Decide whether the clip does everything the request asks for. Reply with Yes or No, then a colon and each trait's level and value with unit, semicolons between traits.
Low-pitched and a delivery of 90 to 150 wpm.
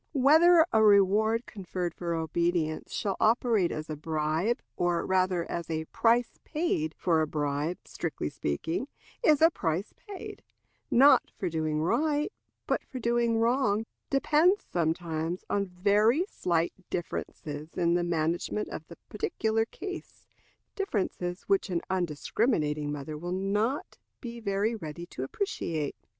No: medium, 185 Hz; slow, 135 wpm